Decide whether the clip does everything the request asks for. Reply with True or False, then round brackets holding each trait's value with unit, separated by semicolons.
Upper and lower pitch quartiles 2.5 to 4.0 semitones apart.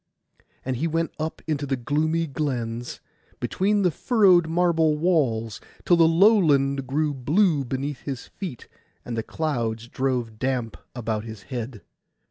False (5.1 semitones)